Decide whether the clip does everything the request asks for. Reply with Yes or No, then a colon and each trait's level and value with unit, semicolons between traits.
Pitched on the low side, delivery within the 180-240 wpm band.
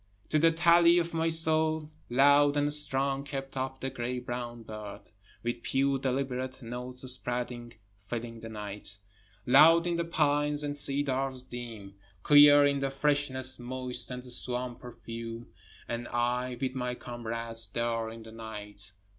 No: low, 130 Hz; average, 155 wpm